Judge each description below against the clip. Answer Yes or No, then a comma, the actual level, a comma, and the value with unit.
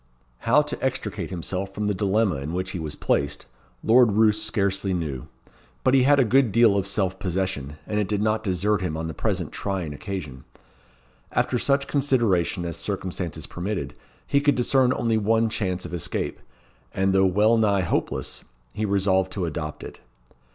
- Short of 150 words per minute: No, average, 175 wpm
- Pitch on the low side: Yes, low, 100 Hz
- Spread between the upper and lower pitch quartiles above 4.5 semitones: No, average, 3.7 semitones